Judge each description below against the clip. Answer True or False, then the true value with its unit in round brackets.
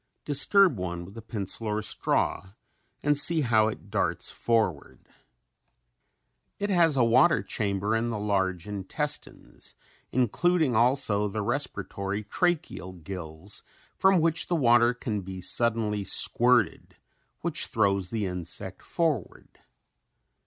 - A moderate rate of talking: False (120 wpm)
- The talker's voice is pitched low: True (110 Hz)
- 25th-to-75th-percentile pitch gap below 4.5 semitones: False (5.3 semitones)